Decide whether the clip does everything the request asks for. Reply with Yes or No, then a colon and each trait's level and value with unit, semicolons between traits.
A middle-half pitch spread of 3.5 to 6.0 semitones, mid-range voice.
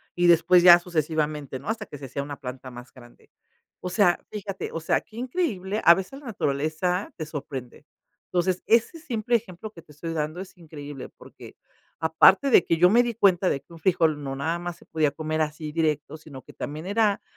Yes: average, 4.2 semitones; medium, 165 Hz